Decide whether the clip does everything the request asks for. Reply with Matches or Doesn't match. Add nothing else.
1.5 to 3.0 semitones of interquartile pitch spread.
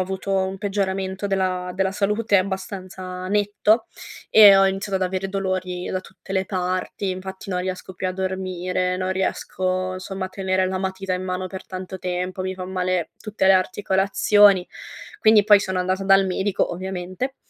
Doesn't match